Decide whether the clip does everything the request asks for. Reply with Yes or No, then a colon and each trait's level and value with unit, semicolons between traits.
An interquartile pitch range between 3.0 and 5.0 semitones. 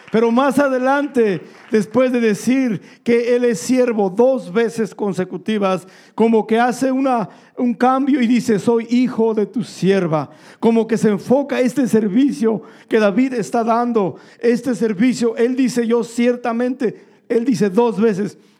No: narrow, 2.4 semitones